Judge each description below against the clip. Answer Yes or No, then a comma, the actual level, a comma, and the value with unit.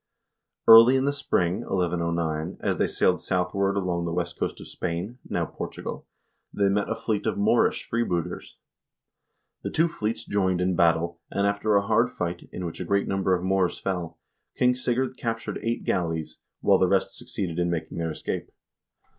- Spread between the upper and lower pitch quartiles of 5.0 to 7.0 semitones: No, average, 4.5 semitones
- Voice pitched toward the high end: No, very low, 95 Hz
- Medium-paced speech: Yes, average, 175 wpm